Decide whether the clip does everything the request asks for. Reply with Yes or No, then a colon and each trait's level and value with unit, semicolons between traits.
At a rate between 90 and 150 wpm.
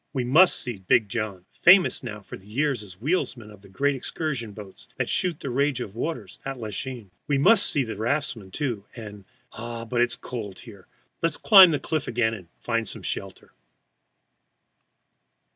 No: average, 180 wpm